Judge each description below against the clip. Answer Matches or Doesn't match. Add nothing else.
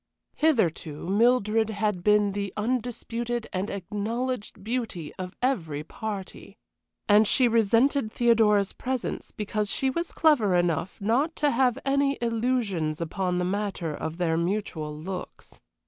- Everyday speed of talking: Doesn't match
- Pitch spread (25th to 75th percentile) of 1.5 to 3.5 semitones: Doesn't match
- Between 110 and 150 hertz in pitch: Doesn't match